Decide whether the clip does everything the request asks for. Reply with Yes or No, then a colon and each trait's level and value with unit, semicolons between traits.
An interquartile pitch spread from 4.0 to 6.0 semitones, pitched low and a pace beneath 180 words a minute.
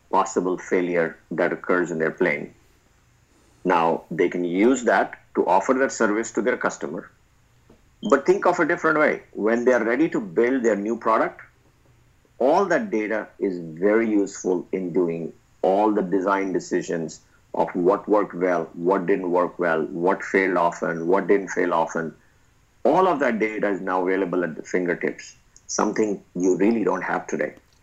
Yes: average, 5.2 semitones; low, 105 Hz; average, 165 wpm